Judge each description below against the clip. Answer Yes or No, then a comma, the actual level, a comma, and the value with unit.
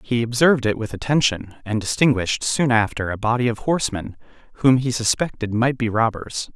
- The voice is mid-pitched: No, low, 115 Hz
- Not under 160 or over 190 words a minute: Yes, average, 175 wpm